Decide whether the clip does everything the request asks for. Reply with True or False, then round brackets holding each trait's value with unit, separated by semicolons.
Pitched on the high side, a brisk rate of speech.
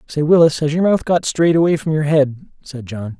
False (150 Hz; 245 wpm)